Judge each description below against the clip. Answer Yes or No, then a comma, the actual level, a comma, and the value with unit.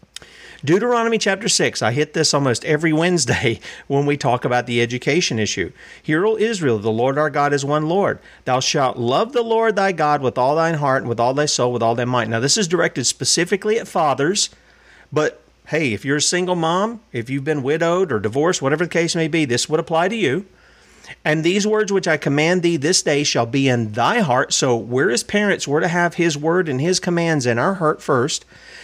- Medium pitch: Yes, medium, 155 Hz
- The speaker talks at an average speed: No, fast, 220 wpm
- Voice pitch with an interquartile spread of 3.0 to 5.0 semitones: No, wide, 5.6 semitones